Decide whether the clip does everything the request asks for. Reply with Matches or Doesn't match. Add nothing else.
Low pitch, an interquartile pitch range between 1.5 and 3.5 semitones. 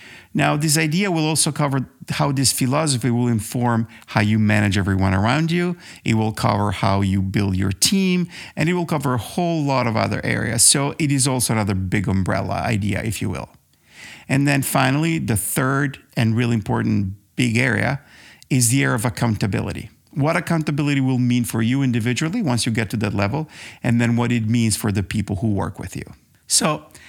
Doesn't match